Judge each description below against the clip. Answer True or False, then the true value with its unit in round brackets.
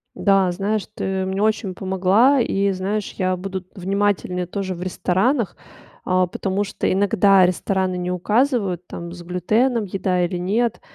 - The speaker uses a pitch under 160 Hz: False (190 Hz)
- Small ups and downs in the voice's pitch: True (2.1 semitones)